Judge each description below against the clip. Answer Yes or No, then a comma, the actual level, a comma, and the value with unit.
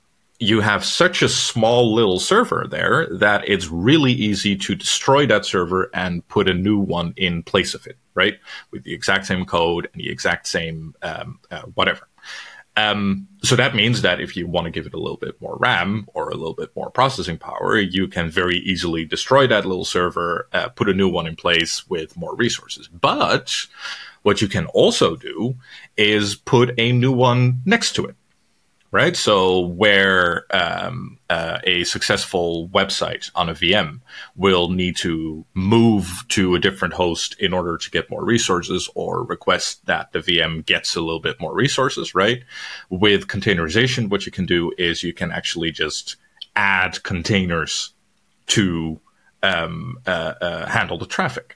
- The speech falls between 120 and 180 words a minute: Yes, average, 175 wpm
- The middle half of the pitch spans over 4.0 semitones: No, average, 3.5 semitones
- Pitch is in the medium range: No, very low, 95 Hz